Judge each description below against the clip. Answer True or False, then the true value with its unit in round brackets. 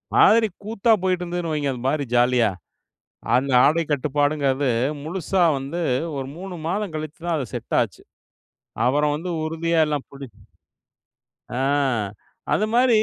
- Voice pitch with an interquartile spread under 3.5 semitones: False (4.3 semitones)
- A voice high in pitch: False (155 Hz)